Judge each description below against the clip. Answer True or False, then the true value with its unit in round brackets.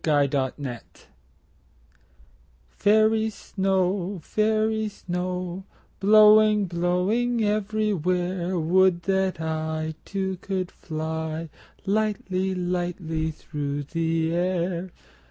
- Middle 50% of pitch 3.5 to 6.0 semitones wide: True (3.8 semitones)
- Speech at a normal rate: False (80 wpm)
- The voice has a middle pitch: True (180 Hz)